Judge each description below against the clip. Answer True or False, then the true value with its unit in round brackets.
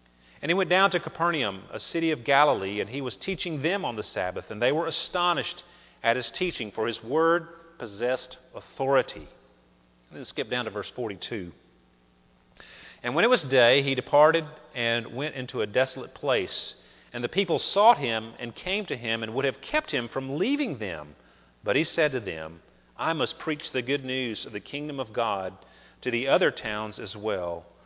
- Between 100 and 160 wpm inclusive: False (190 wpm)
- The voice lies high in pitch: False (130 Hz)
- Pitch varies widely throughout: True (8.4 semitones)